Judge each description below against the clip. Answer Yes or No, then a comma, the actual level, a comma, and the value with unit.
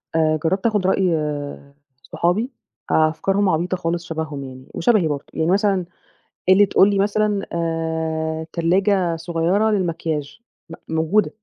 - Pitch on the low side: No, medium, 170 Hz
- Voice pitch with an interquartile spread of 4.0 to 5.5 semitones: No, average, 3.5 semitones